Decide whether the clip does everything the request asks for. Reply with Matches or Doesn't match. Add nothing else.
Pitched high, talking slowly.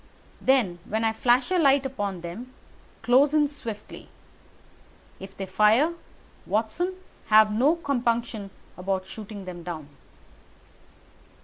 Matches